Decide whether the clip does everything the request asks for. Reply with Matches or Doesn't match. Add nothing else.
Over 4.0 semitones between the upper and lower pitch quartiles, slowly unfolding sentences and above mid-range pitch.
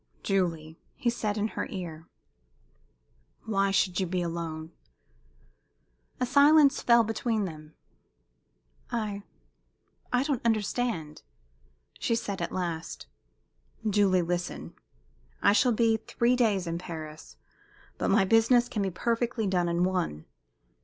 Matches